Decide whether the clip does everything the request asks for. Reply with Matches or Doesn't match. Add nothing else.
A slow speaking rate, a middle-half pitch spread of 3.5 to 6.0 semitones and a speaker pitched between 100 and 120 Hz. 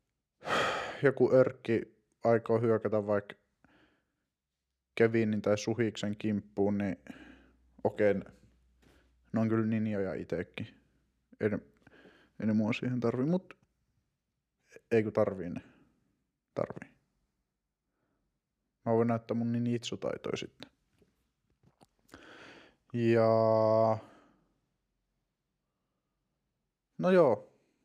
Doesn't match